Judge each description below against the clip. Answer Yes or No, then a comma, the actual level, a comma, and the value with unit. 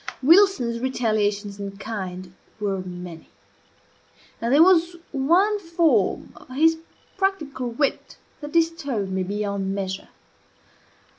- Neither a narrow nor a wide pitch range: No, wide, 8.5 semitones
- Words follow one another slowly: Yes, slow, 105 wpm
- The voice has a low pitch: No, high, 235 Hz